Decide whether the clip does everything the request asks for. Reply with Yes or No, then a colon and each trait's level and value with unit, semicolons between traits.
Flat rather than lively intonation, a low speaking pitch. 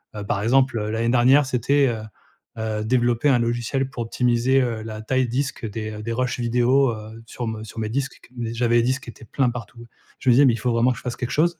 Yes: narrow, 2.3 semitones; low, 120 Hz